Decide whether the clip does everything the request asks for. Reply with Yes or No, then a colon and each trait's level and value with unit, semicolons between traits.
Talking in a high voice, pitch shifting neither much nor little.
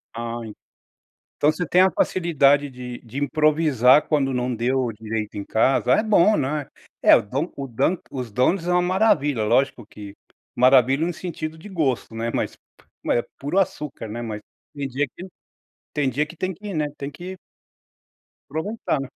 No: medium, 140 Hz; average, 5.0 semitones